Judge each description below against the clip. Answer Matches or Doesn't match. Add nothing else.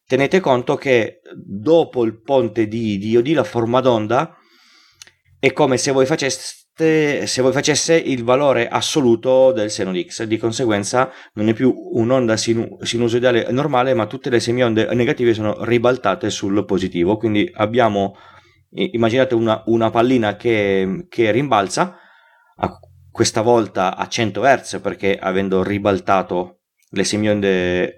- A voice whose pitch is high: Doesn't match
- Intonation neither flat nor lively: Matches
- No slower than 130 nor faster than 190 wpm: Matches